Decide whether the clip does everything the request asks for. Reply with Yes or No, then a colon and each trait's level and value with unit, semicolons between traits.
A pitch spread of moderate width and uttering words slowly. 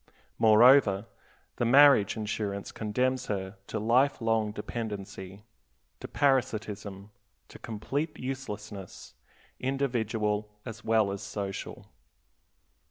Yes: average, 3.6 semitones; slow, 95 wpm